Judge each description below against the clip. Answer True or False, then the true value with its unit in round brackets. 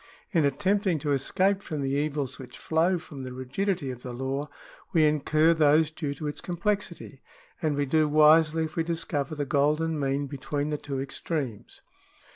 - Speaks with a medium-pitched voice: True (150 Hz)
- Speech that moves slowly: False (175 wpm)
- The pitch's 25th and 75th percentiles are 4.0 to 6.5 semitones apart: False (2.7 semitones)